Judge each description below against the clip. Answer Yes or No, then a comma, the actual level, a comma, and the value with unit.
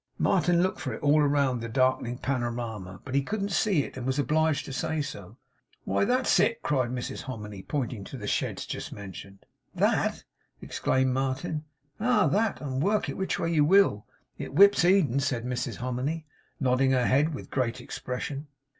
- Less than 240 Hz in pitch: Yes, low, 135 Hz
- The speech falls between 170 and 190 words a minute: Yes, average, 180 wpm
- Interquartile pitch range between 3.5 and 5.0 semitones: Yes, average, 4.4 semitones